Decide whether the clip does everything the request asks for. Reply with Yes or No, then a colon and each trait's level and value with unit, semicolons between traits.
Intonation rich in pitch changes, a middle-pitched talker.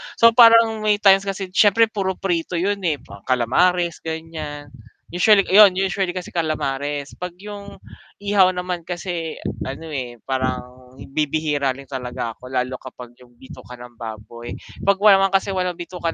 Yes: wide, 6.5 semitones; medium, 170 Hz